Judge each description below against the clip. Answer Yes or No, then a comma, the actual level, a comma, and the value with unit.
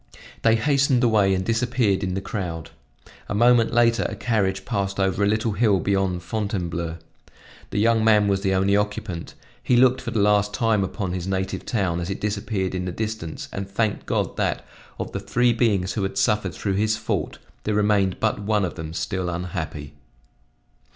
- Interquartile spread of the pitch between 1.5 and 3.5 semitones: Yes, average, 2.8 semitones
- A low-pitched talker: Yes, low, 100 Hz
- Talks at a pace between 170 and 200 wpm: Yes, average, 185 wpm